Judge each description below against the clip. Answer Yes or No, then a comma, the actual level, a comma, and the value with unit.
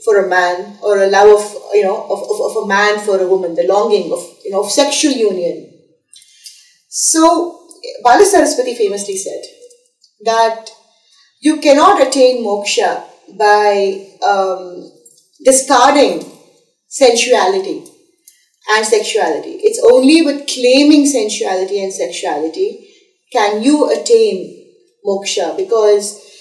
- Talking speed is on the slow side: Yes, slow, 120 wpm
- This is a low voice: No, very high, 260 Hz